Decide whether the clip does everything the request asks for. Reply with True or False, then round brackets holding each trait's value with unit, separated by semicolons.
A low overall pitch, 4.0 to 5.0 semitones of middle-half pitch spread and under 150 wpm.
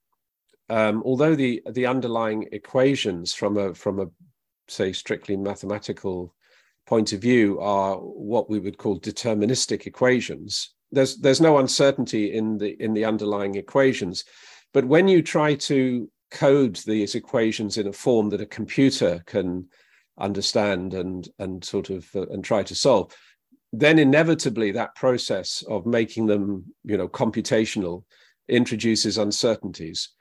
True (110 Hz; 4.4 semitones; 140 wpm)